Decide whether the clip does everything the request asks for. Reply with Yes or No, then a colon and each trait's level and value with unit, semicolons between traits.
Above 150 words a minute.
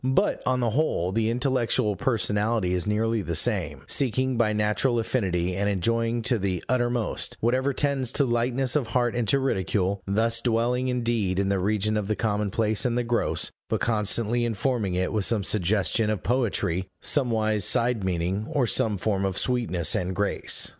Yes: average, 175 wpm